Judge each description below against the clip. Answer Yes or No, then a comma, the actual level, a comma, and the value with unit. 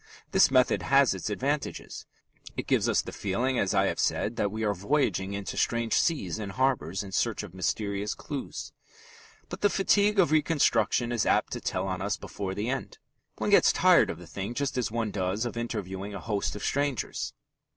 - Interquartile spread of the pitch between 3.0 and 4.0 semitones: No, average, 5.1 semitones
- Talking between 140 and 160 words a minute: No, average, 195 wpm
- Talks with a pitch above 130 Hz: No, low, 110 Hz